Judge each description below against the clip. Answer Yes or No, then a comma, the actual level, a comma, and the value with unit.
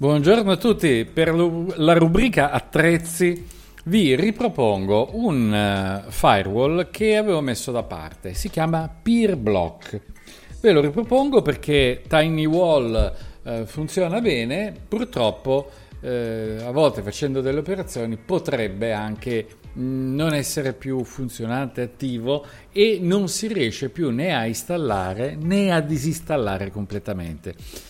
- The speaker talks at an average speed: No, slow, 110 wpm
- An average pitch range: No, wide, 7.4 semitones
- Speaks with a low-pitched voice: No, medium, 145 Hz